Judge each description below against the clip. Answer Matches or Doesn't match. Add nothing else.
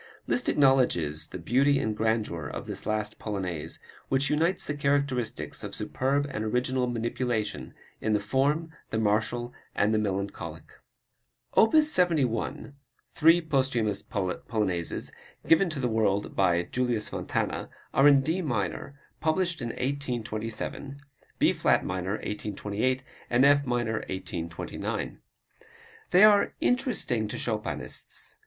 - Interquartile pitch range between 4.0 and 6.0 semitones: Matches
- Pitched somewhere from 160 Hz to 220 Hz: Doesn't match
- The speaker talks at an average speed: Doesn't match